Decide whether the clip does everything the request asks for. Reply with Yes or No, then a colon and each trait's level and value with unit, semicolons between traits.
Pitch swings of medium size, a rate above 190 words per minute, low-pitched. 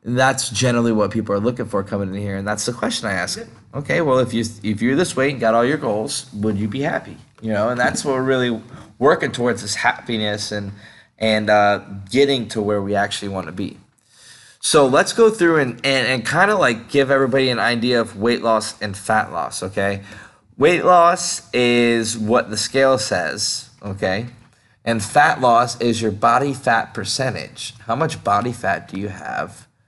Yes: average, 3.7 semitones; average, 200 wpm; low, 115 Hz